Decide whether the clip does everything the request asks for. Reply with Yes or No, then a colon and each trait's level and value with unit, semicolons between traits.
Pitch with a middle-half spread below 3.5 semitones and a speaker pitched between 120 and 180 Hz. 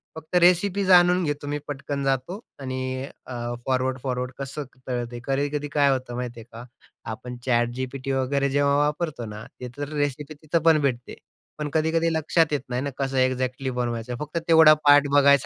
Yes: average, 2.8 semitones; medium, 140 Hz